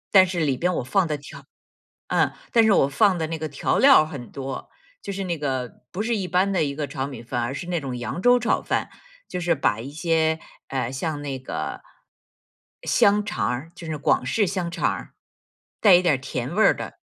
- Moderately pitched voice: Yes, medium, 160 Hz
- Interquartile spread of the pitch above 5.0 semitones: Yes, wide, 5.4 semitones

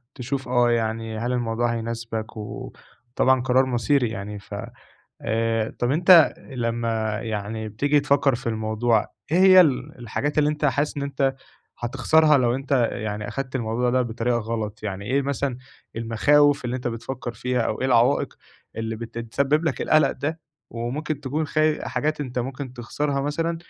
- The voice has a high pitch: No, low, 125 Hz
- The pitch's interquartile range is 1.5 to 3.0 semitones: No, average, 3.7 semitones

